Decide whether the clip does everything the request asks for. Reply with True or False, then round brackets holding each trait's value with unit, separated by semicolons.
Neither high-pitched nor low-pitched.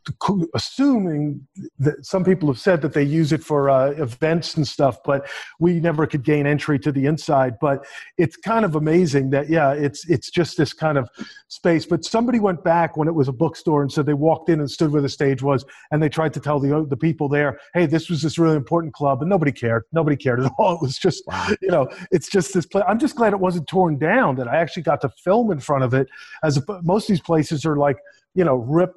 True (155 Hz)